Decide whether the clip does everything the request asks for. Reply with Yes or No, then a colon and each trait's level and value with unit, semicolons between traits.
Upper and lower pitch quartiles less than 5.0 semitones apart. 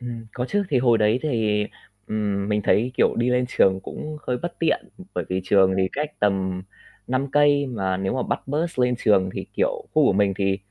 No: wide, 5.4 semitones